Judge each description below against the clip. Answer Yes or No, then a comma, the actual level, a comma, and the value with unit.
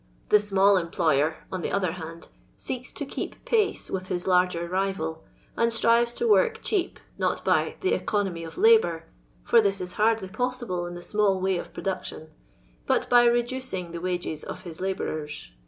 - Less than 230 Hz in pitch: Yes, high, 190 Hz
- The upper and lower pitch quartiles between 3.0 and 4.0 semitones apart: No, average, 5.2 semitones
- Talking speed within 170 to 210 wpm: Yes, average, 175 wpm